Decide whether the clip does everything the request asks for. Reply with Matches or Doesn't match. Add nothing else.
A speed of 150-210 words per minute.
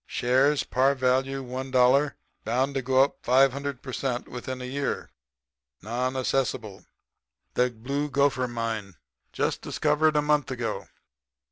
Doesn't match